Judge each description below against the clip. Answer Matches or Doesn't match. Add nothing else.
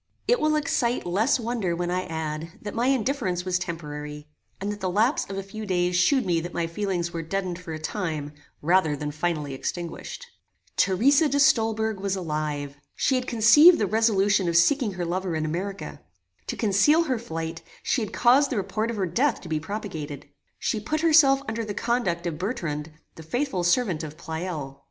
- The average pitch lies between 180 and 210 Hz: Matches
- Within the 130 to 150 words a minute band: Doesn't match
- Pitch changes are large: Matches